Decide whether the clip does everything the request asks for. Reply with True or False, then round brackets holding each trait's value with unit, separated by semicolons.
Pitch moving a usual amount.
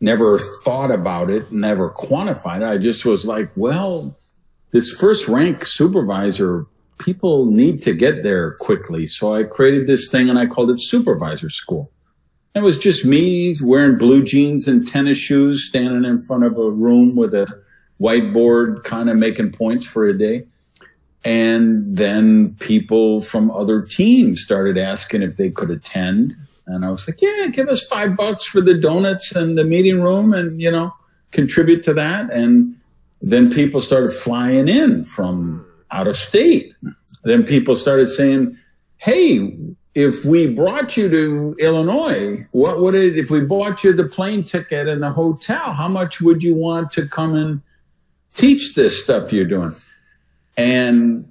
False (7.8 semitones)